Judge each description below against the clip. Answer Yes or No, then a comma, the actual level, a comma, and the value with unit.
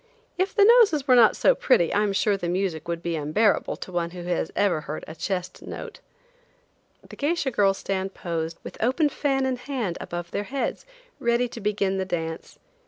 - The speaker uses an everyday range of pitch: No, wide, 6.7 semitones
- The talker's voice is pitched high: Yes, high, 195 Hz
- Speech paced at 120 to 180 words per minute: No, average, 195 wpm